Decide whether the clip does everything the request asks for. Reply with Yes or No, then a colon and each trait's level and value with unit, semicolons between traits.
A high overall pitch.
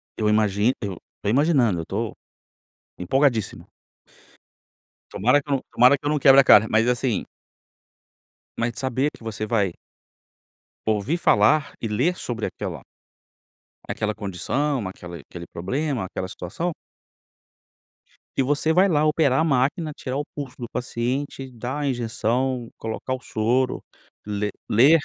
No: low, 125 Hz